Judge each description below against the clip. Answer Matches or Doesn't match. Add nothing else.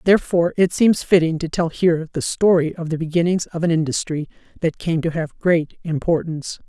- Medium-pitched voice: Matches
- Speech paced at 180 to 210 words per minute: Matches